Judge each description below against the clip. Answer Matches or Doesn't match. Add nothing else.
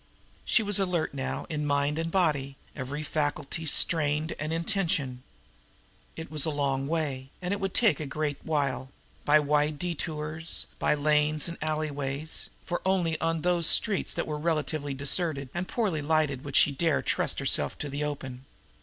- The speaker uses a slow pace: Doesn't match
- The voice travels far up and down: Doesn't match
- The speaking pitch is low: Doesn't match